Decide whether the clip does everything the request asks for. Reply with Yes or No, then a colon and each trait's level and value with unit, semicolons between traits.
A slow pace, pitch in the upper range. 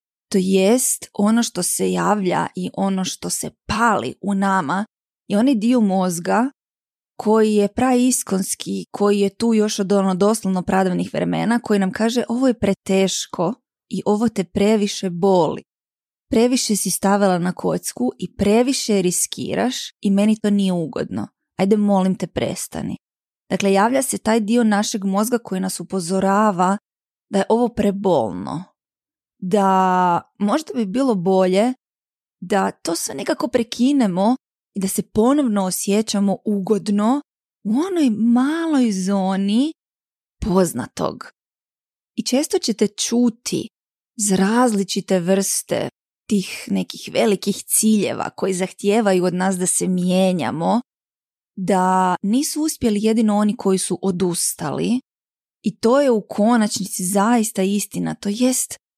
No: average, 130 wpm; high, 205 Hz